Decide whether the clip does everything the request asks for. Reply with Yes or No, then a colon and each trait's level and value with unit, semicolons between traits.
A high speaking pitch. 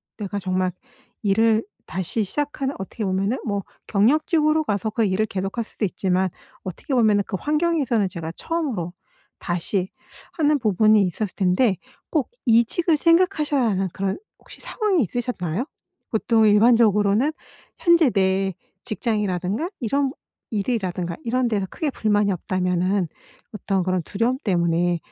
Yes: high, 210 Hz